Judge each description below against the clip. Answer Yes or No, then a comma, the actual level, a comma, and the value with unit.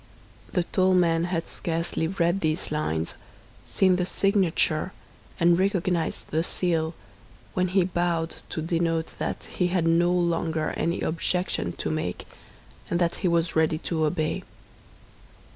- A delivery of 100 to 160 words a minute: Yes, average, 140 wpm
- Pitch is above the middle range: No, medium, 170 Hz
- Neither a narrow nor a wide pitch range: No, narrow, 1.7 semitones